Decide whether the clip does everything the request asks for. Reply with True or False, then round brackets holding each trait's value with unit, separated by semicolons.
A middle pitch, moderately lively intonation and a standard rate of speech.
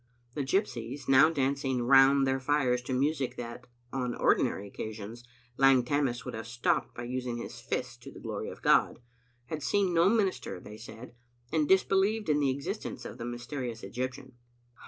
False (130 Hz; 3.2 semitones; 170 wpm)